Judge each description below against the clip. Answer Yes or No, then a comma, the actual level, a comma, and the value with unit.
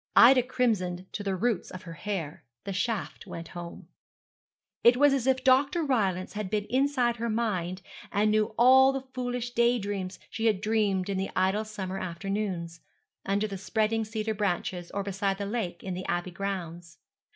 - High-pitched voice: Yes, high, 205 Hz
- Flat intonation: No, average, 4.2 semitones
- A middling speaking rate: Yes, average, 175 wpm